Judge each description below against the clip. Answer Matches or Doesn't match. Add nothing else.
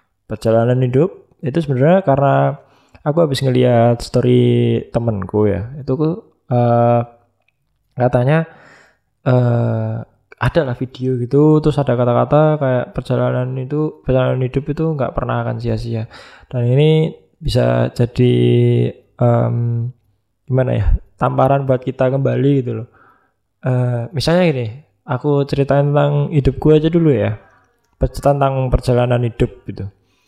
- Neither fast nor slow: Matches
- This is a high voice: Doesn't match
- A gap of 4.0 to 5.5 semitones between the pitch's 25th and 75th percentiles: Doesn't match